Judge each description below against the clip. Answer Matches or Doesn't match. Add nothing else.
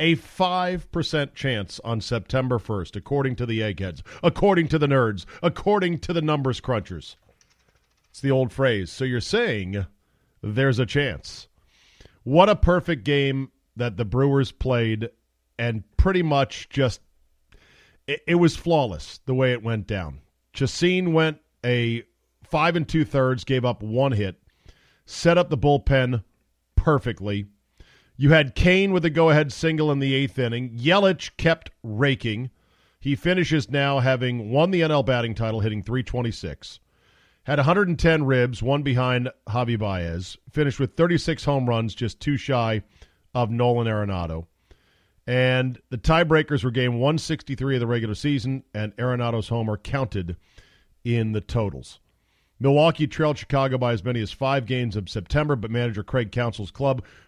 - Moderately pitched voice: Doesn't match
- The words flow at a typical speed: Matches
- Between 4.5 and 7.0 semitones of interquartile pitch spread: Matches